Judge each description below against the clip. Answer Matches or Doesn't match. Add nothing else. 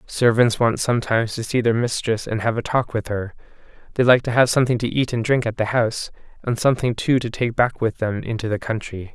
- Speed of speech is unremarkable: Doesn't match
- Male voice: Matches